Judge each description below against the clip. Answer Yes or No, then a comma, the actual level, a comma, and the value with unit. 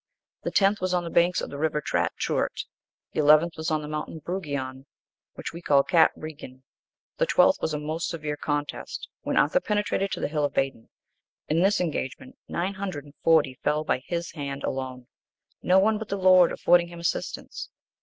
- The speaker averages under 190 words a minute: No, average, 195 wpm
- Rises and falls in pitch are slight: No, average, 3.7 semitones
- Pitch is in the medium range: Yes, medium, 160 Hz